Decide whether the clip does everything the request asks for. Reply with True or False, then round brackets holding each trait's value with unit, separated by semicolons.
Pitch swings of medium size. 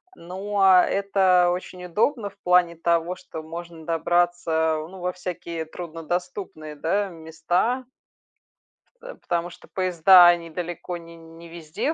False (1.9 semitones)